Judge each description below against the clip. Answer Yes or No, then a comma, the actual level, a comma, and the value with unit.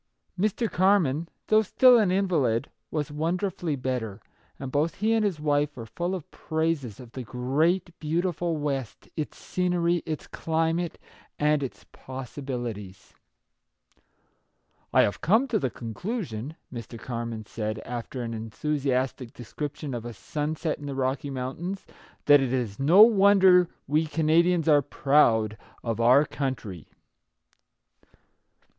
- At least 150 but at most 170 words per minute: No, average, 140 wpm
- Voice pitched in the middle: Yes, medium, 145 Hz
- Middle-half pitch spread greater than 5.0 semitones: Yes, wide, 5.6 semitones